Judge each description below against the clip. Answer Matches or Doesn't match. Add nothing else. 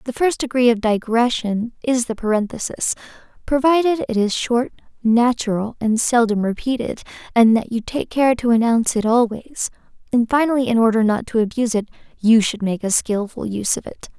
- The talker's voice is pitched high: Matches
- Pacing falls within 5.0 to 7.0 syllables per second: Matches